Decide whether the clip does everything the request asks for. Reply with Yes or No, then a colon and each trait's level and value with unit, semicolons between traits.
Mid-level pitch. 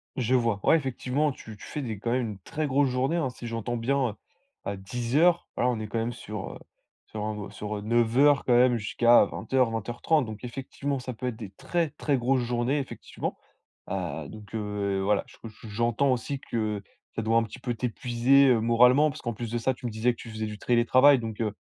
No: low, 120 Hz